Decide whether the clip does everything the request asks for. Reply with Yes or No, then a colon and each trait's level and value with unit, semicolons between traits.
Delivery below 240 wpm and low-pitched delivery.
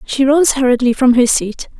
No: average, 200 wpm; very high, 260 Hz